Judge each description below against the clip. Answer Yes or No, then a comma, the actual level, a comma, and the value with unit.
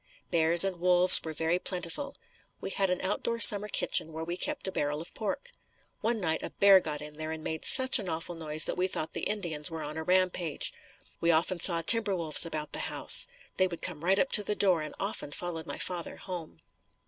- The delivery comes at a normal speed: No, fast, 220 wpm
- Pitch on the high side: No, medium, 175 Hz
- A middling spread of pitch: Yes, average, 3.4 semitones